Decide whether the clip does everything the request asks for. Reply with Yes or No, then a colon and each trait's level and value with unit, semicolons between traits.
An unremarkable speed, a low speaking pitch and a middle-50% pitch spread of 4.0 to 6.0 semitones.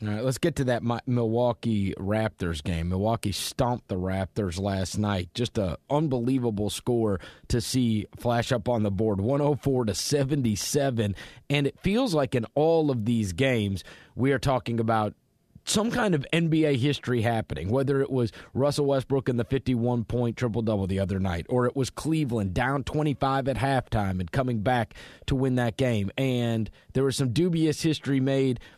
Yes: average, 170 wpm; low, 120 Hz; average, 4.3 semitones